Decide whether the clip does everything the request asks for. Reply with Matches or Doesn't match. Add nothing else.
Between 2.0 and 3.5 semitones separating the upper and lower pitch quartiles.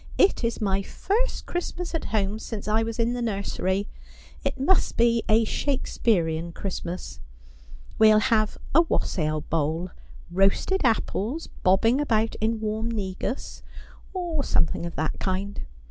Doesn't match